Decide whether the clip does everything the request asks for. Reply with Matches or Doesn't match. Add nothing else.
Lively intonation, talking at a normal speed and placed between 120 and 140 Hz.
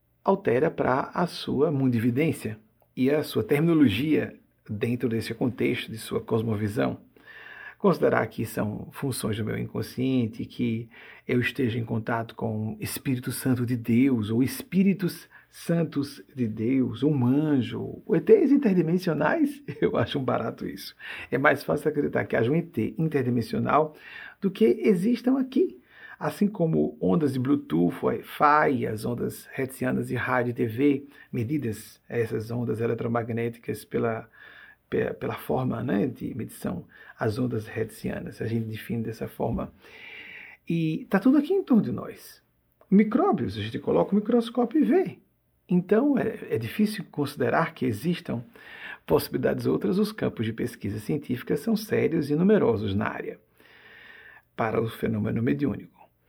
Matches